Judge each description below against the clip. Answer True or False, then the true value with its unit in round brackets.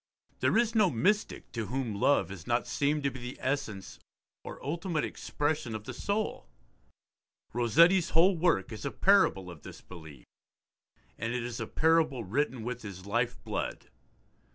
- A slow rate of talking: False (160 wpm)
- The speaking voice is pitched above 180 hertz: False (125 Hz)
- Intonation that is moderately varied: False (7.0 semitones)